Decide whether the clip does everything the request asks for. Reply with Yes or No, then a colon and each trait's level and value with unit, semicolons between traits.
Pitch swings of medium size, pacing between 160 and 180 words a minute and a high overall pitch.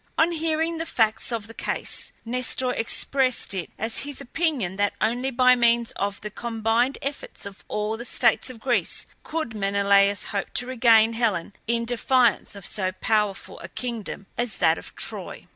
Yes: average, 3.4 semitones; average, 170 wpm; high, 230 Hz